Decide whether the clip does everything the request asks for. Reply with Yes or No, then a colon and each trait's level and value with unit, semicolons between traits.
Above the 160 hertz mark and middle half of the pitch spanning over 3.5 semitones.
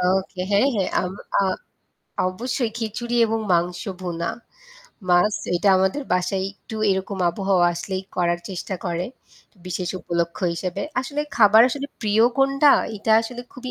Yes: high, 190 Hz; average, 3.9 semitones